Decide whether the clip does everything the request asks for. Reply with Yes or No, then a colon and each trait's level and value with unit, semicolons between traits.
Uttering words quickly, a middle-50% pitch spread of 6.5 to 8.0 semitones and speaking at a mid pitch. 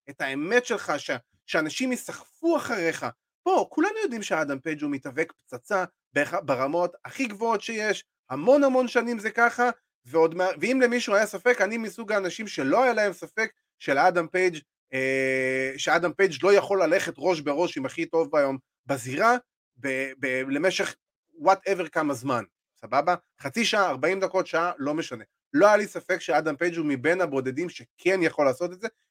Yes: fast, 165 wpm; wide, 7.0 semitones; medium, 180 Hz